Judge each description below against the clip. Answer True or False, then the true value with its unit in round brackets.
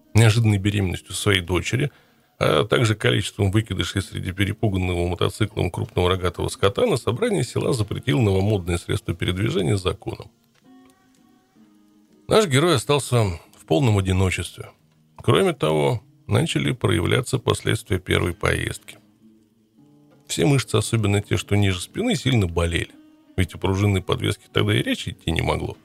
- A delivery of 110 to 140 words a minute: True (125 wpm)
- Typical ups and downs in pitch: True (3.6 semitones)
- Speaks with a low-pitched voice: True (105 Hz)